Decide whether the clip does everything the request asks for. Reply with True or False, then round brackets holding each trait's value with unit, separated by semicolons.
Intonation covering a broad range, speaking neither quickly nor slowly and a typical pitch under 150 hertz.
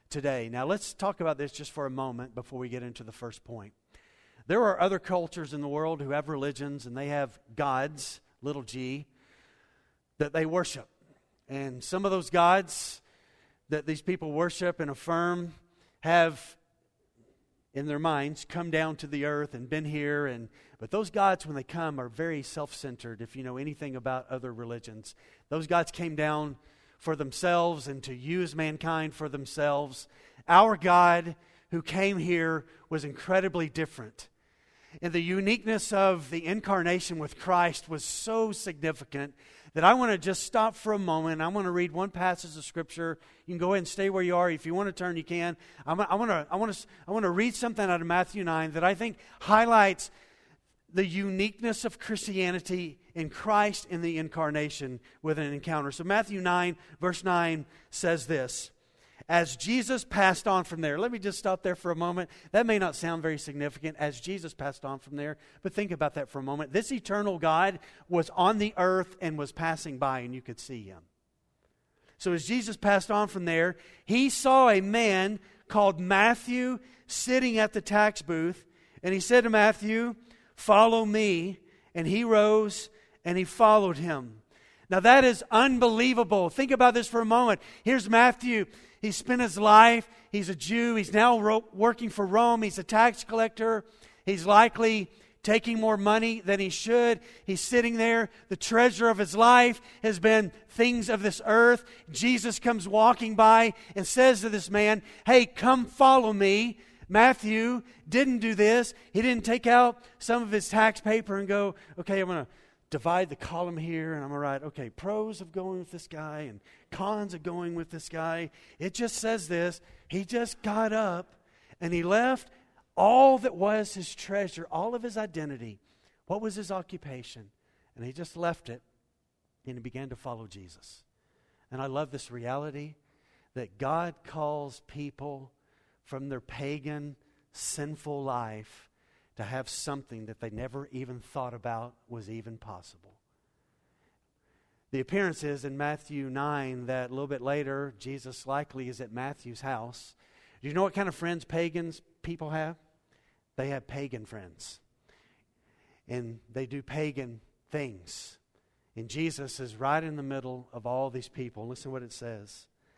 False (6.6 semitones; 175 wpm; 170 Hz)